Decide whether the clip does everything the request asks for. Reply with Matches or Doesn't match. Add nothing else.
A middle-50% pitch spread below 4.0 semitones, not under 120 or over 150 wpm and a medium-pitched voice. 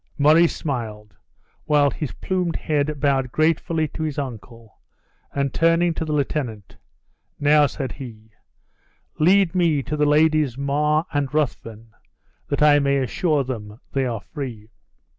Matches